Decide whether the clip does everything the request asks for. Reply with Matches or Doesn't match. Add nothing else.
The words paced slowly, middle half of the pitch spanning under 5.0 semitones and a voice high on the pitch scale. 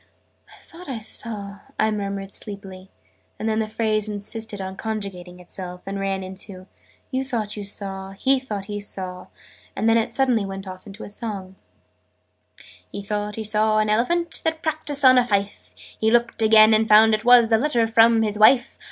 Doesn't match